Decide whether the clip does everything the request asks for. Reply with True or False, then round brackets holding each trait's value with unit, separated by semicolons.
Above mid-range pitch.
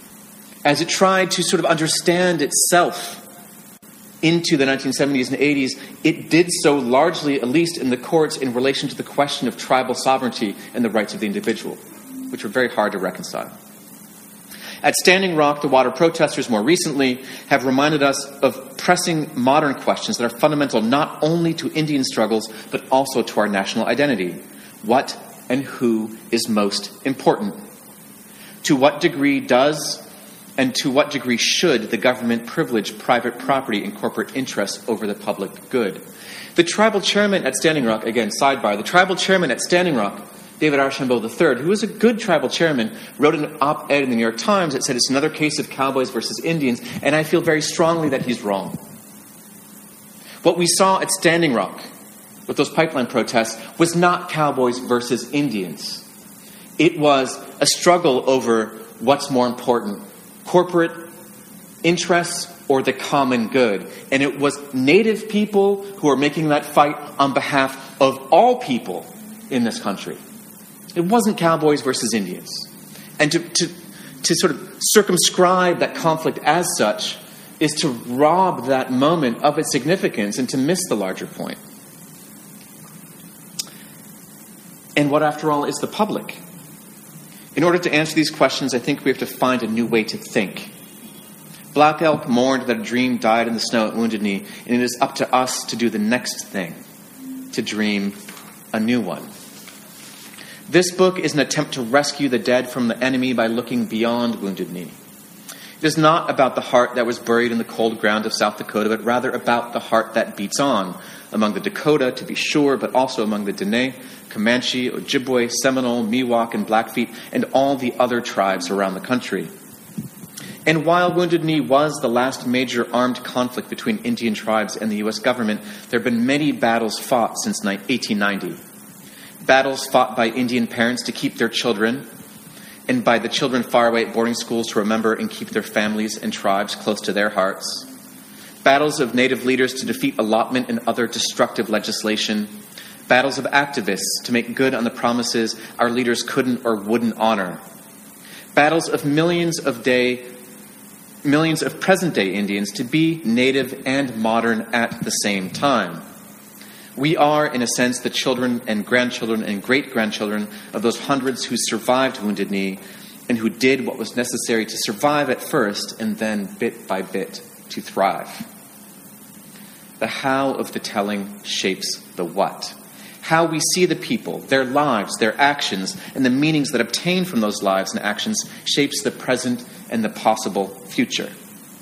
False (135 Hz)